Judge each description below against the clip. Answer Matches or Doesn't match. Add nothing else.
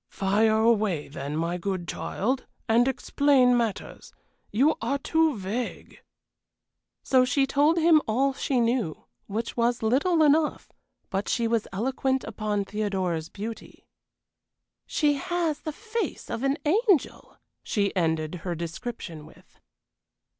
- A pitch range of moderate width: Doesn't match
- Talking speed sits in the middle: Doesn't match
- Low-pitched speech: Doesn't match